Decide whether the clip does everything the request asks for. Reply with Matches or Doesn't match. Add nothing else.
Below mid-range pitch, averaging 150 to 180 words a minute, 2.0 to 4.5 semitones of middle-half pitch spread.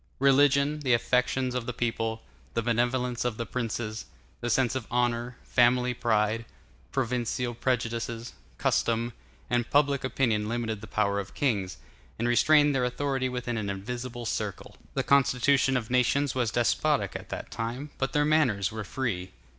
Matches